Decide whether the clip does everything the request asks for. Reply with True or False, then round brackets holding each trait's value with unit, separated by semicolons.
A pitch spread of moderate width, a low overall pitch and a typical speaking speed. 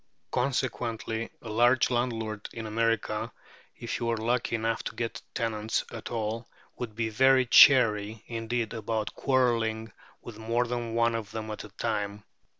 False (1.4 semitones; 115 Hz; 150 wpm)